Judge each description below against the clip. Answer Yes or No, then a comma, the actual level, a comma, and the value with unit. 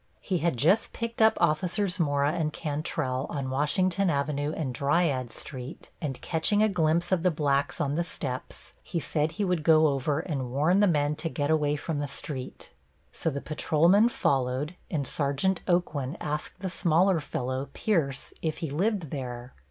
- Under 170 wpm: No, average, 175 wpm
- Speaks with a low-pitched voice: No, medium, 155 Hz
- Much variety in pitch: No, average, 3.7 semitones